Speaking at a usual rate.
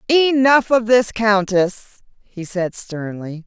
No: slow, 120 wpm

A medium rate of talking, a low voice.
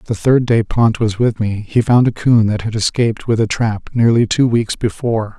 No: fast, 235 wpm; low, 110 Hz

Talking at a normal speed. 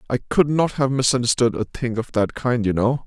No: fast, 235 wpm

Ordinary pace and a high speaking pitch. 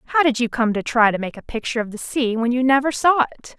No: fast, 300 wpm; high, 245 Hz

